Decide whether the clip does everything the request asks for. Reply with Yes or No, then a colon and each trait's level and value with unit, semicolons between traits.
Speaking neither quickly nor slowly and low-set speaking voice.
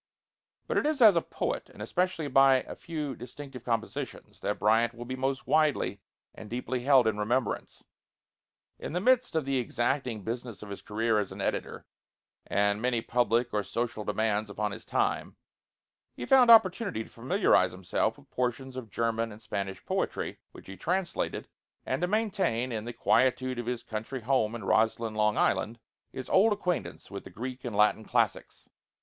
Yes: average, 175 wpm; low, 120 Hz